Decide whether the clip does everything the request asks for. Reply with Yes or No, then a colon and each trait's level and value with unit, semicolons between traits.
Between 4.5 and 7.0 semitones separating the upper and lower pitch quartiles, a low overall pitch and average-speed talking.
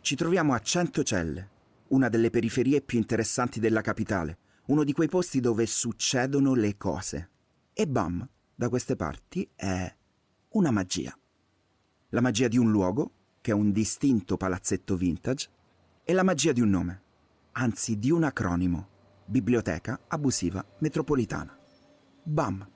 Yes: wide, 5.5 semitones; low, 115 Hz; average, 135 wpm